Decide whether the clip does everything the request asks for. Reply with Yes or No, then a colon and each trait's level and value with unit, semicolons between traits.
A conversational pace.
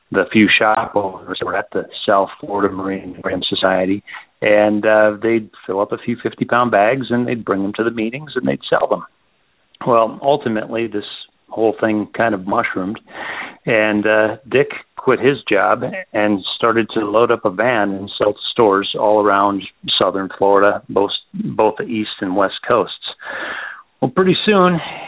Yes: average, 170 wpm